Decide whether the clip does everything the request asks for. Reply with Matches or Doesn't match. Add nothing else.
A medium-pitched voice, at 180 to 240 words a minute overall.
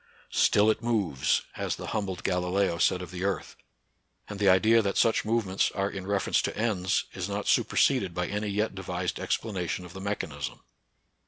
Doesn't match